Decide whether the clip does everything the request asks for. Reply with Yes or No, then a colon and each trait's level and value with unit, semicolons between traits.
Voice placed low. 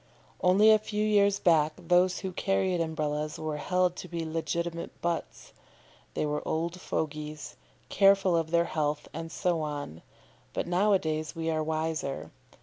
No: medium, 165 Hz